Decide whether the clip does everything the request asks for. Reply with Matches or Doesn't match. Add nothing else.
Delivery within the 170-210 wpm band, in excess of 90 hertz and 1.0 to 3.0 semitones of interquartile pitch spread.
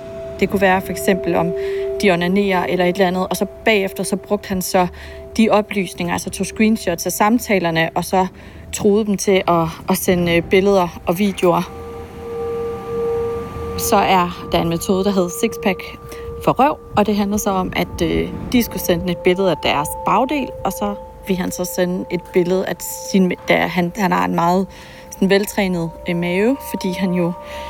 Matches